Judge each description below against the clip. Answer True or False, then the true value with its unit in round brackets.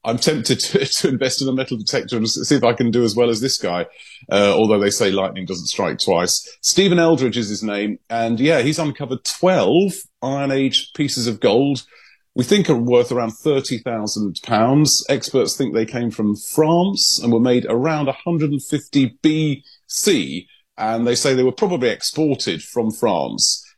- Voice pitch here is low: True (130 Hz)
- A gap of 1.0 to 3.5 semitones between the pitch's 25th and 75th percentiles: False (4.6 semitones)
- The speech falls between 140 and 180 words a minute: False (190 wpm)